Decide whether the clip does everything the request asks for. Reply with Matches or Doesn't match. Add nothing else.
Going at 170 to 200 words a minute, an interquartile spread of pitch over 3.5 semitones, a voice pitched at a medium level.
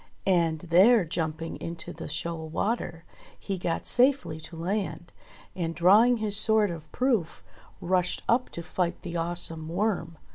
Doesn't match